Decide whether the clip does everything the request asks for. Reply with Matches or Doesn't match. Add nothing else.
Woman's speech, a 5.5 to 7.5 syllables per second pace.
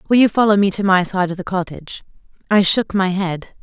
Matches